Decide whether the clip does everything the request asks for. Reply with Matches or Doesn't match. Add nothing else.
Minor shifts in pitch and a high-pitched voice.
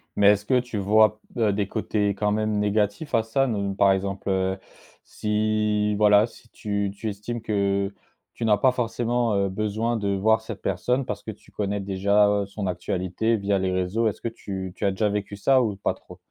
Doesn't match